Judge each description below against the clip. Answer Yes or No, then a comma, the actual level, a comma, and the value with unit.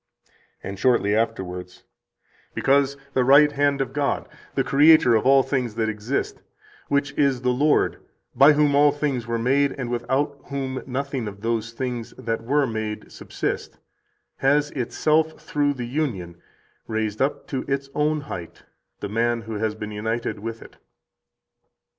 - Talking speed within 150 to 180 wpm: Yes, average, 155 wpm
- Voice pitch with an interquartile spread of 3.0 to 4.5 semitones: Yes, average, 3.9 semitones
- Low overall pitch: Yes, low, 130 Hz